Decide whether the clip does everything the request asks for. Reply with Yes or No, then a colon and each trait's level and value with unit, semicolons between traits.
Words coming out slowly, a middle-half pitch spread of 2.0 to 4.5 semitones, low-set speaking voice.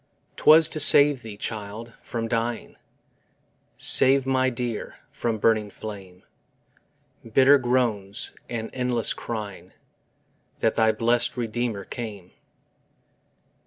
Yes: slow, 100 wpm; average, 2.7 semitones; low, 115 Hz